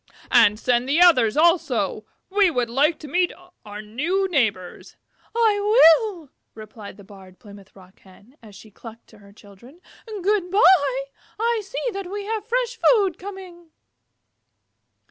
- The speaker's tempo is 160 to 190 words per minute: No, average, 145 wpm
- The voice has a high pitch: Yes, very high, 305 Hz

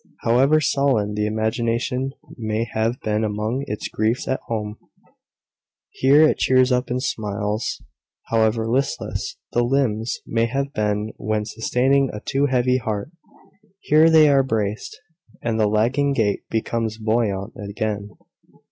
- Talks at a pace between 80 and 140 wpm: Yes, slow, 135 wpm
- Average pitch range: Yes, average, 3.4 semitones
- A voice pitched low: Yes, low, 115 Hz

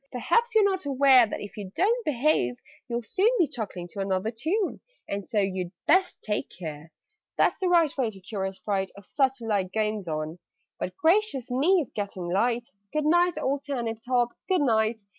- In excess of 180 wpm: Yes, average, 190 wpm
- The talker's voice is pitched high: Yes, high, 240 Hz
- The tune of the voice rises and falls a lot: Yes, wide, 7.6 semitones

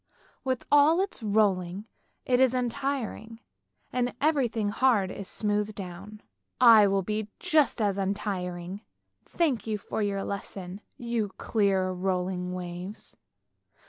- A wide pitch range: No, average, 4.2 semitones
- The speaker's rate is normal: No, slow, 125 wpm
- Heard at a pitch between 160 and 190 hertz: No, high, 210 Hz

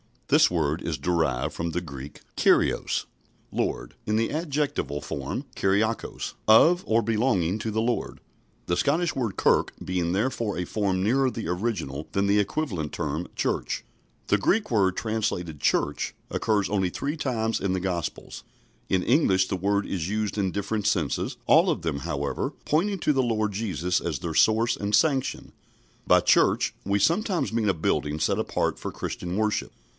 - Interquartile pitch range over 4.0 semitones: Yes, average, 4.7 semitones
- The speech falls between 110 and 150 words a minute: No, average, 165 wpm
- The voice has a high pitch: No, low, 100 Hz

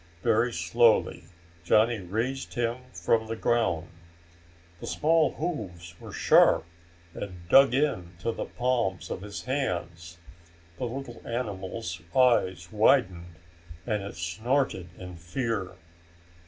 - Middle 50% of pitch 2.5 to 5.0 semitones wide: No, wide, 5.5 semitones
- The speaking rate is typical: No, slow, 115 wpm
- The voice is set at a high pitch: No, low, 110 Hz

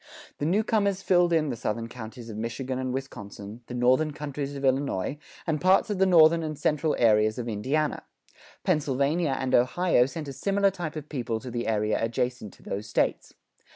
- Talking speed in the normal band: Yes, average, 185 wpm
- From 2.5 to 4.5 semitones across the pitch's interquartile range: No, average, 5.1 semitones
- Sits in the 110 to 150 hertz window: Yes, low, 135 Hz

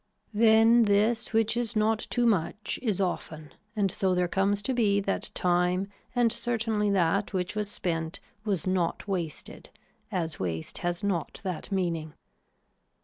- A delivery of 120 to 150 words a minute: Yes, average, 145 wpm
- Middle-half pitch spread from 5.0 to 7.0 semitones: No, average, 3.8 semitones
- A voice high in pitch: Yes, high, 200 Hz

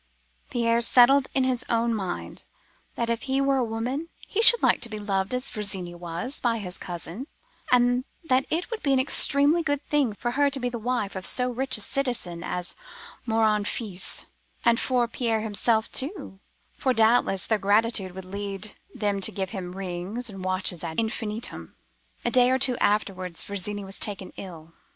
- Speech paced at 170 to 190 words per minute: Yes, average, 180 wpm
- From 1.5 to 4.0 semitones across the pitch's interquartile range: No, average, 4.6 semitones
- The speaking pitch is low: No, high, 225 Hz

